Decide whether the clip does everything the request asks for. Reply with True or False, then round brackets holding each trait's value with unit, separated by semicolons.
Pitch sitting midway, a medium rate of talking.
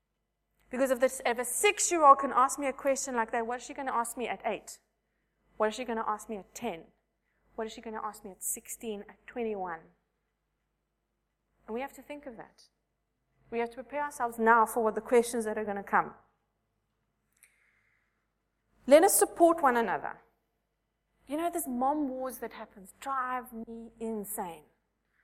False (240 Hz; 190 wpm)